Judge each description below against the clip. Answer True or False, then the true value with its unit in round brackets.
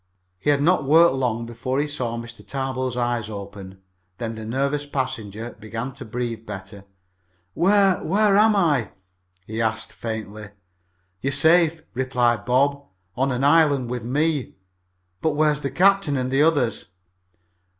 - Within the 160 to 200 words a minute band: False (150 wpm)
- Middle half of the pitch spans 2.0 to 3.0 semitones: False (4.4 semitones)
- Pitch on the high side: False (130 Hz)